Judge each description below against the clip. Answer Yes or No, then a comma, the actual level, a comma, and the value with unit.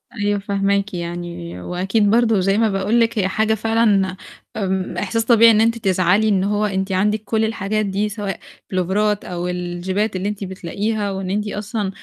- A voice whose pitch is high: Yes, high, 200 Hz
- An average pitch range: No, narrow, 2.3 semitones